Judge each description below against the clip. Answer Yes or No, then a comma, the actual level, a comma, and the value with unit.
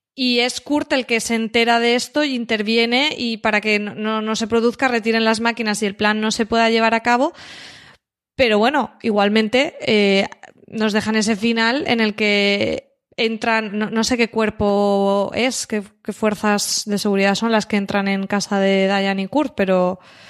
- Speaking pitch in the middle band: No, high, 220 Hz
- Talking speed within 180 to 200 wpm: Yes, fast, 190 wpm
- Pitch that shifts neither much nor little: No, narrow, 2.2 semitones